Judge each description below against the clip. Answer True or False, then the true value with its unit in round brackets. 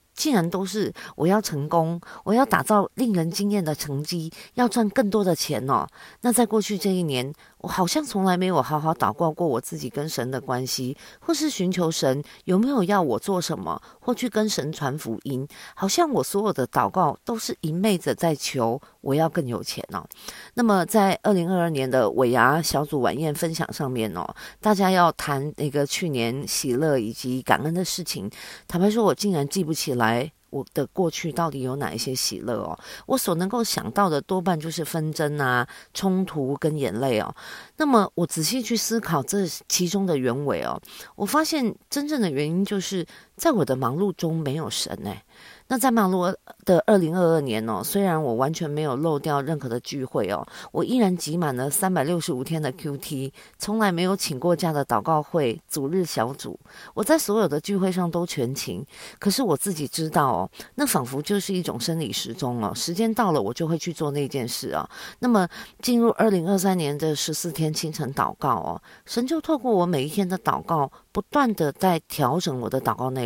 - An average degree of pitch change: False (5.9 semitones)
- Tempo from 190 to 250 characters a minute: False (285 characters per minute)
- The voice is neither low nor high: True (170 Hz)